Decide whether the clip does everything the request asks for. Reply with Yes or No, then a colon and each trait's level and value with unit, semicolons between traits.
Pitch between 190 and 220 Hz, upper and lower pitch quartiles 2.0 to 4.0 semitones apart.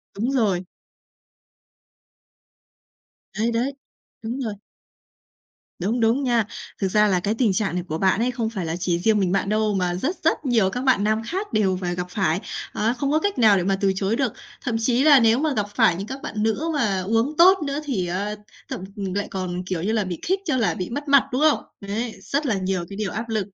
No: high, 215 Hz; average, 4.8 semitones